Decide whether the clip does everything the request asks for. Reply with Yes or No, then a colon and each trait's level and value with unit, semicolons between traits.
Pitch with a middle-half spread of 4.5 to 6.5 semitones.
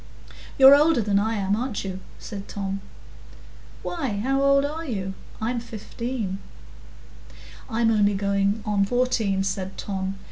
No: average, 4.1 semitones